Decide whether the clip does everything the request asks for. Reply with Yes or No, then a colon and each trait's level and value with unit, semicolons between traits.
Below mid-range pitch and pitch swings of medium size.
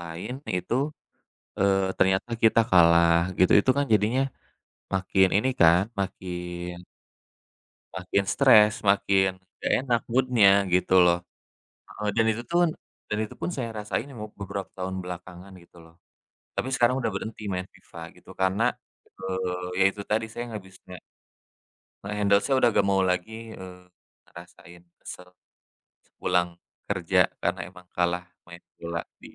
Yes: very low, 95 Hz; average, 3.2 semitones